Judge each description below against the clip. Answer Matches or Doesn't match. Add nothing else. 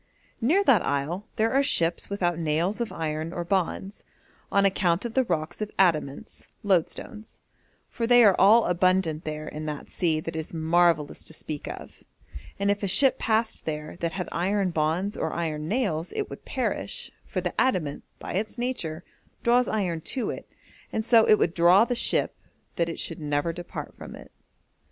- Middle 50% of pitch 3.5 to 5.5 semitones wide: Matches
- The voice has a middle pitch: Matches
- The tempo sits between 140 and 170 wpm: Doesn't match